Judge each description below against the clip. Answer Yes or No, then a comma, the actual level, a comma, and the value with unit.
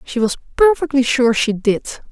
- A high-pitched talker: Yes, very high, 255 Hz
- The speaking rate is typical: Yes, average, 170 wpm